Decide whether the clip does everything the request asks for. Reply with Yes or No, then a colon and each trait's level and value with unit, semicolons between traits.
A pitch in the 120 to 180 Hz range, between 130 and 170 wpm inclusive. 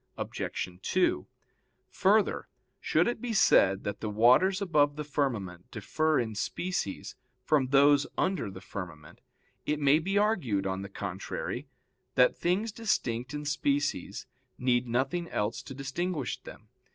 Yes: medium, 140 Hz; average, 140 wpm